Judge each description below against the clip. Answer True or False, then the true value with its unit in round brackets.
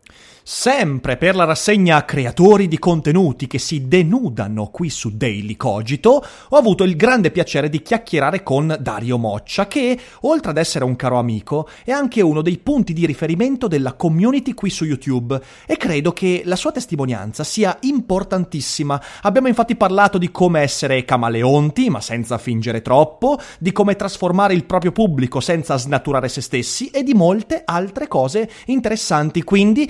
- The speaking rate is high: False (160 wpm)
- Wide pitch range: True (7.3 semitones)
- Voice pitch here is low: False (170 Hz)